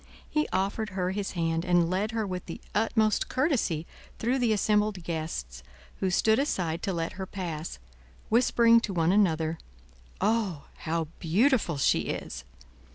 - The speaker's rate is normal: Yes, average, 150 wpm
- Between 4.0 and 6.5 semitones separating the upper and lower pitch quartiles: Yes, average, 4.8 semitones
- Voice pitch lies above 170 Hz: Yes, high, 190 Hz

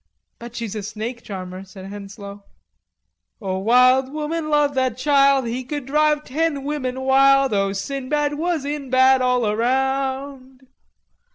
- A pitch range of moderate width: Yes, average, 3.8 semitones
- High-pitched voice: Yes, very high, 260 Hz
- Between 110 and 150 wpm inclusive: Yes, average, 140 wpm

